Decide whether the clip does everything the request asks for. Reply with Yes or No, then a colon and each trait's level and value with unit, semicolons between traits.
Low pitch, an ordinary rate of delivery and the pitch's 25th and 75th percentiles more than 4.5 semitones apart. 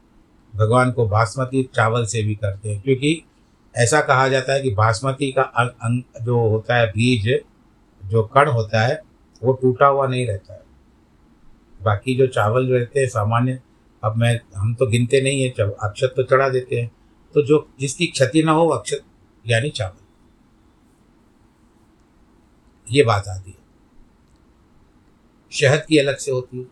No: low, 120 Hz; average, 155 wpm; average, 3.7 semitones